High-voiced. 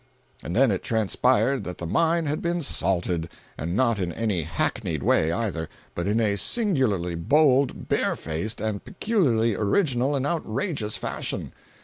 No: low, 110 Hz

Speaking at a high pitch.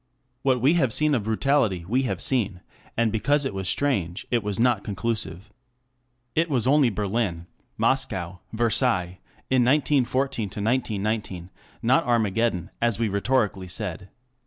No: low, 115 Hz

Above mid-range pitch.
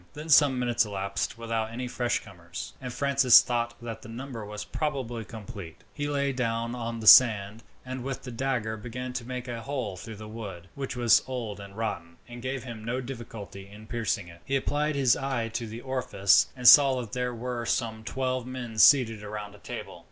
No: low, 120 Hz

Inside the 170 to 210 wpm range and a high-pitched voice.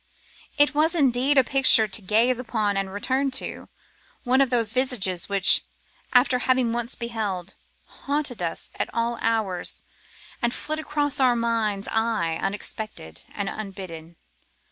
No: average, 145 wpm; high, 230 Hz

